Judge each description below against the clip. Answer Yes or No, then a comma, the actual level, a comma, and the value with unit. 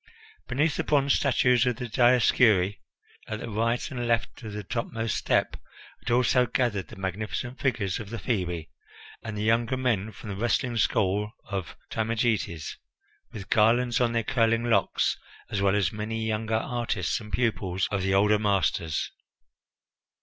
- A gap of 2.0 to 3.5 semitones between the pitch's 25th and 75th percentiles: Yes, average, 2.9 semitones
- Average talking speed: Yes, average, 155 wpm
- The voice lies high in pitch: No, low, 110 Hz